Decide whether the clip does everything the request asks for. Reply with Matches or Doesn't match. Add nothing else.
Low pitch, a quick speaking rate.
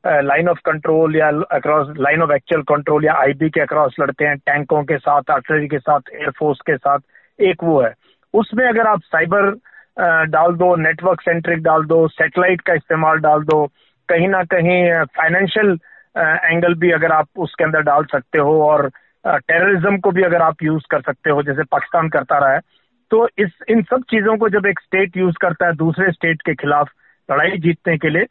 Doesn't match